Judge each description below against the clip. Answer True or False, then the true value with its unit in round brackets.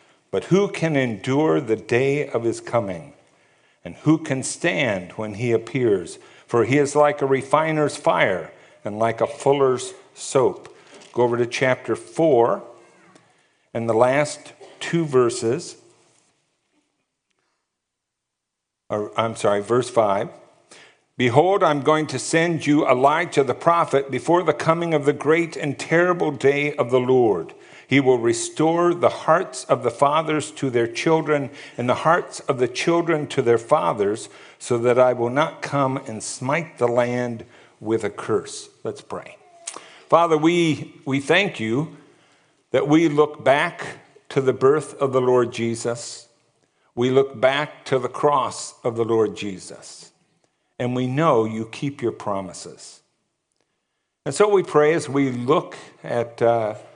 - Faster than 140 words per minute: True (150 wpm)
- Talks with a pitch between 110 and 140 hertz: True (135 Hz)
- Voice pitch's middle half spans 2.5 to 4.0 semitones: False (4.5 semitones)